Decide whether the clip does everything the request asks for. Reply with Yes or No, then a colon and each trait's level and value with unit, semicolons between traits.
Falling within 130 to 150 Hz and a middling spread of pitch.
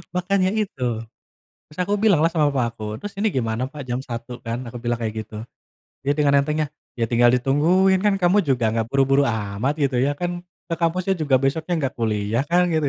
No: medium, 140 Hz; wide, 6.6 semitones